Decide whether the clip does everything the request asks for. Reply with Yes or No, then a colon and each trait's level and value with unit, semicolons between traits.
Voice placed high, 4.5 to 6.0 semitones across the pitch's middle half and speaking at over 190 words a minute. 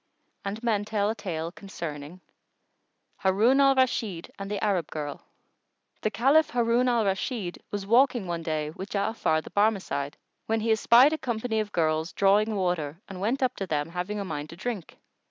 No: high, 200 Hz; average, 4.9 semitones; average, 175 wpm